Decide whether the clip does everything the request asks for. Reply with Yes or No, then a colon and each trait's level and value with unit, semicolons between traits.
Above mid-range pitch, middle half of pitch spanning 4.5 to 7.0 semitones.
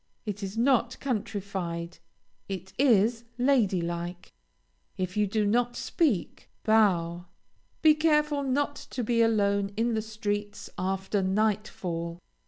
No: high, 210 Hz; average, 4.1 semitones